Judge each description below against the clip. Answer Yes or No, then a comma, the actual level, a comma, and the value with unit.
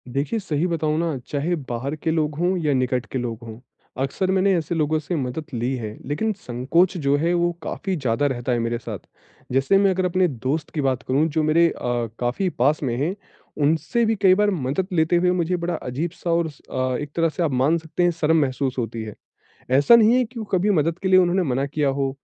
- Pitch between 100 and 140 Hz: No, medium, 155 Hz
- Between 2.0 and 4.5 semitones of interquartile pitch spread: No, average, 4.9 semitones